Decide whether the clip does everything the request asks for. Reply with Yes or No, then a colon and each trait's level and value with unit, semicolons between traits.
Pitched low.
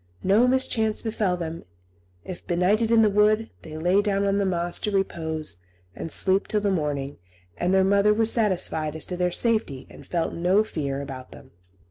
No: high, 190 Hz